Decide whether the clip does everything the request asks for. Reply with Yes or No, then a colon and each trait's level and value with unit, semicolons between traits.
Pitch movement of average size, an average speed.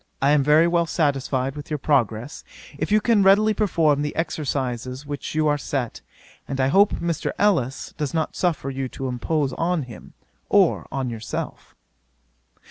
Yes: average, 3.9 semitones; average, 165 wpm